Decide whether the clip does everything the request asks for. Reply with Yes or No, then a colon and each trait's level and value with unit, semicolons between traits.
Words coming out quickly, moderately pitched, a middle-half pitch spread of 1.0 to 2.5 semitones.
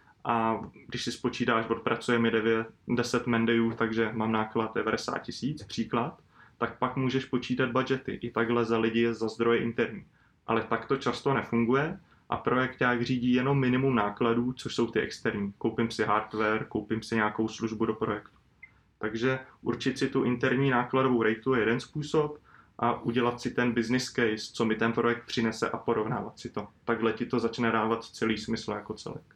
No: fast, 180 wpm; low, 115 Hz; narrow, 2.1 semitones